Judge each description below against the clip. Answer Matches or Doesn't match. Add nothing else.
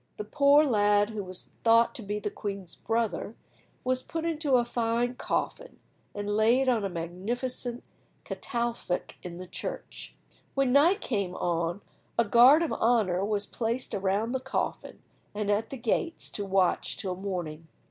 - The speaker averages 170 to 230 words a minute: Doesn't match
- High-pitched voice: Matches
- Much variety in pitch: Doesn't match